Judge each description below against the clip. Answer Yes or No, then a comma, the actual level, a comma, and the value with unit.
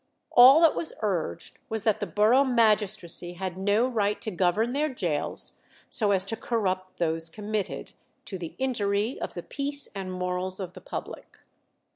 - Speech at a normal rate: Yes, average, 165 wpm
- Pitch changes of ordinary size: Yes, average, 4.0 semitones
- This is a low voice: No, high, 205 Hz